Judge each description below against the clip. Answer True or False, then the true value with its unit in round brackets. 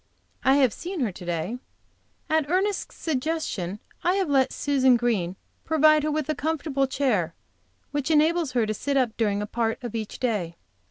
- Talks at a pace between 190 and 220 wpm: False (175 wpm)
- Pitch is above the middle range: True (265 Hz)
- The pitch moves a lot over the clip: True (5.8 semitones)